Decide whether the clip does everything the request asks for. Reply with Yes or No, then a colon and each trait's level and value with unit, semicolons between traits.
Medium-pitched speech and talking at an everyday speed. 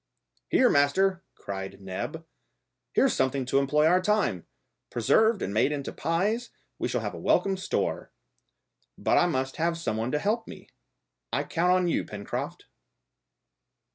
Yes: medium, 160 Hz; average, 150 wpm